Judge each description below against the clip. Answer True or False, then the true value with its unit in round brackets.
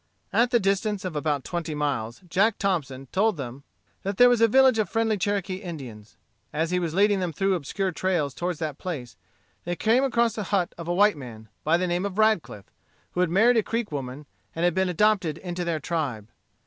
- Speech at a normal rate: False (210 wpm)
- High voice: False (180 Hz)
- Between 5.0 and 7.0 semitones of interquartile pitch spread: True (5.3 semitones)